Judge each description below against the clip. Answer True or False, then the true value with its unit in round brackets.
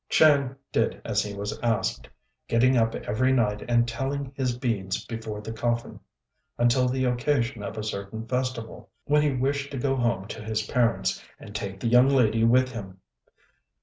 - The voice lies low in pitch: True (120 Hz)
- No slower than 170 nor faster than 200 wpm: True (175 wpm)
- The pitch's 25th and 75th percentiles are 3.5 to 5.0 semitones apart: False (3.1 semitones)